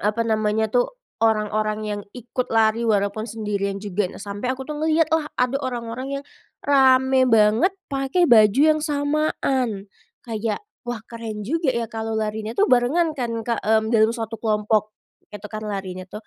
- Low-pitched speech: No, high, 225 Hz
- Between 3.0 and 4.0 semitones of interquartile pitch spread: Yes, average, 3.7 semitones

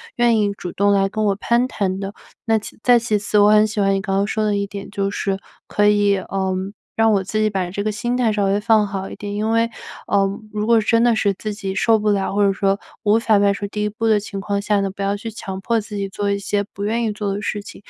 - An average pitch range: No, narrow, 1.5 semitones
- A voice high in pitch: Yes, high, 205 Hz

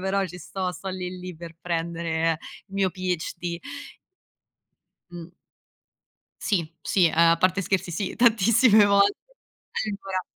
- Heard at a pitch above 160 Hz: Yes, medium, 185 Hz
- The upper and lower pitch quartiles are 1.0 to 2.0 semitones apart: No, average, 2.7 semitones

